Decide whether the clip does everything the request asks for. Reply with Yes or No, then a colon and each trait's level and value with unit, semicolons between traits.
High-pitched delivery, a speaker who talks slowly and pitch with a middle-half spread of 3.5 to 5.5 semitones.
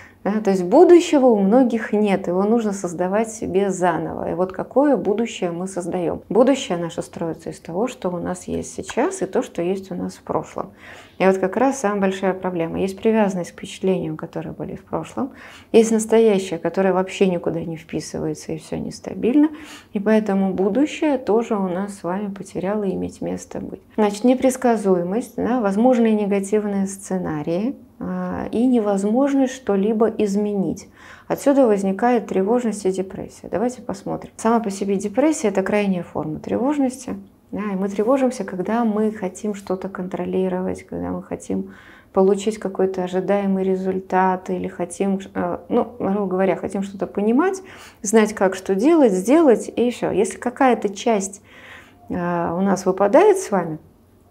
No: high, 200 Hz; average, 150 wpm; average, 4.0 semitones